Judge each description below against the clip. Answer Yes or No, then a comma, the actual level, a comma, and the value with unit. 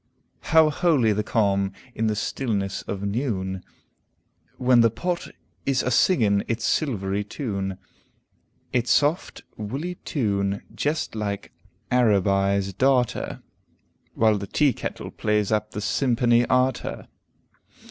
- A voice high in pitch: No, low, 110 Hz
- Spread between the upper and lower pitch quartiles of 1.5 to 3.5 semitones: No, average, 4.4 semitones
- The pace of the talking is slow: Yes, slow, 115 wpm